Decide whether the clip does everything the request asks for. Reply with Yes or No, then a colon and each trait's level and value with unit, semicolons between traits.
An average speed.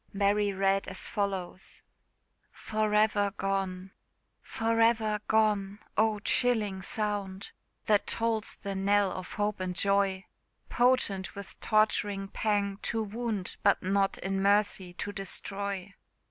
No: slow, 120 wpm